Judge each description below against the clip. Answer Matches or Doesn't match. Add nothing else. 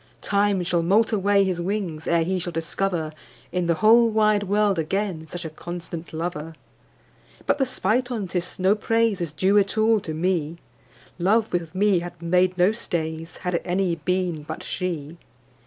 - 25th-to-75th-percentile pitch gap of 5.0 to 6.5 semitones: Doesn't match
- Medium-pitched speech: Matches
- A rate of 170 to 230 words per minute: Matches